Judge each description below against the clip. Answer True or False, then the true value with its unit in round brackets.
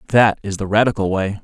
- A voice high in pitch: False (105 Hz)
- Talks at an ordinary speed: False (210 wpm)